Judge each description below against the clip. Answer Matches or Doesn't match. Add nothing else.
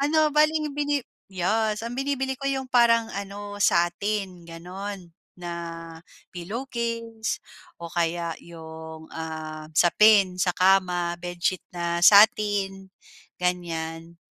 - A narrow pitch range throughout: Doesn't match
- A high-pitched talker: Matches